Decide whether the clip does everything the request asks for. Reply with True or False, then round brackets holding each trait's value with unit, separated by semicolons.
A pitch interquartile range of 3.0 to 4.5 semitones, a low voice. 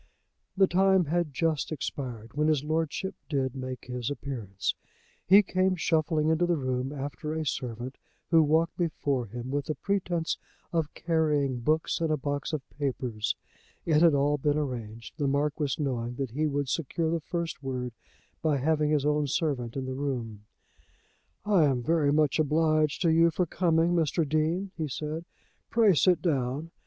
False (3.6 semitones; 150 Hz)